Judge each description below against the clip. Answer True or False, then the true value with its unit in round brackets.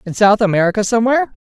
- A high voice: True (215 Hz)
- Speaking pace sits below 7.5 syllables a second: False (8.0 syllables/s)